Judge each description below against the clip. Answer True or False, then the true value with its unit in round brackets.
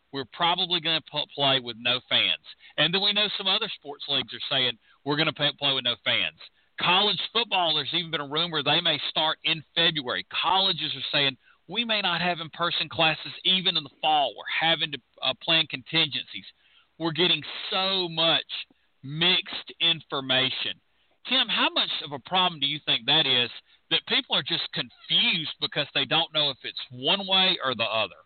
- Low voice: False (160 Hz)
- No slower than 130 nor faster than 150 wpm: False (190 wpm)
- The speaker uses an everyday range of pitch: True (4.1 semitones)